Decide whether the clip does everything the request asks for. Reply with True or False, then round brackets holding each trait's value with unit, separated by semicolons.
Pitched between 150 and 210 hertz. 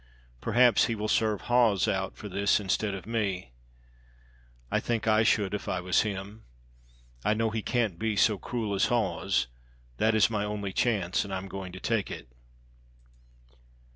False (105 Hz)